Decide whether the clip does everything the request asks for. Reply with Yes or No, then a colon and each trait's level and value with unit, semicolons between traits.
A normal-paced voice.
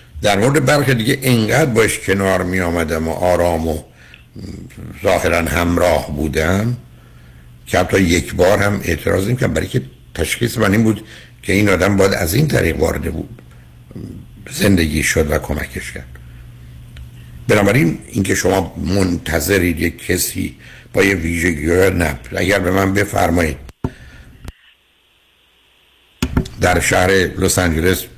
Yes: average, 130 wpm